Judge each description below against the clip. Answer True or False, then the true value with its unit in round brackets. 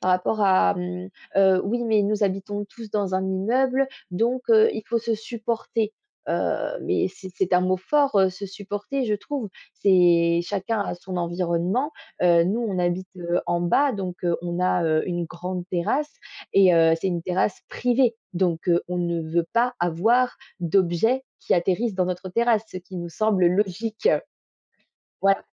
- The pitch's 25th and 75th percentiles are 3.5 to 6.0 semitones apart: True (4.0 semitones)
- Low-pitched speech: False (190 Hz)